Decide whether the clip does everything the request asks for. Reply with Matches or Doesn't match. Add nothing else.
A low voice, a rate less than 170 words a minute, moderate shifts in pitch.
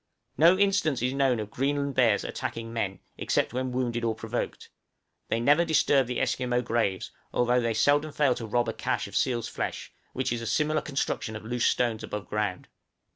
Doesn't match